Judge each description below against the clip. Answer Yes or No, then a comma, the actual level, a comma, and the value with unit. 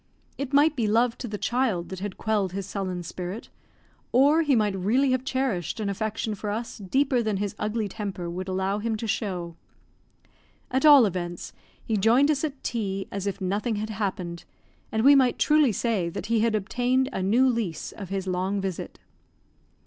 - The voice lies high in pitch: Yes, high, 215 Hz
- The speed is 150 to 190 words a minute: Yes, average, 185 wpm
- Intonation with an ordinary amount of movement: Yes, average, 4.4 semitones